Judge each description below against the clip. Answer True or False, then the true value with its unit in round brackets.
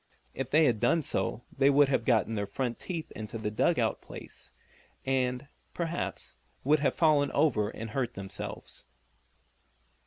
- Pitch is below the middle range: True (130 Hz)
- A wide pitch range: False (4.5 semitones)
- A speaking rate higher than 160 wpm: False (155 wpm)